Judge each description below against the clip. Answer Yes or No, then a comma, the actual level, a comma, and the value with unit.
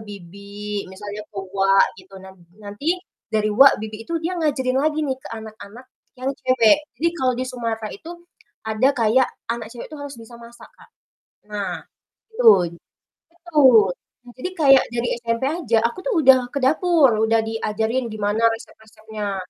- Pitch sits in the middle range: No, high, 230 Hz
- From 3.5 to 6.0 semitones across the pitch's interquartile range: Yes, average, 4.0 semitones